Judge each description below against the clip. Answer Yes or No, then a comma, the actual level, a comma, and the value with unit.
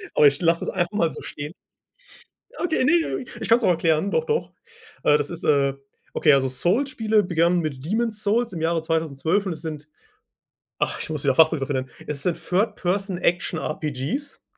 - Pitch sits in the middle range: Yes, medium, 170 Hz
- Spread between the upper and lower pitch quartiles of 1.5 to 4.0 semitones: No, wide, 5.4 semitones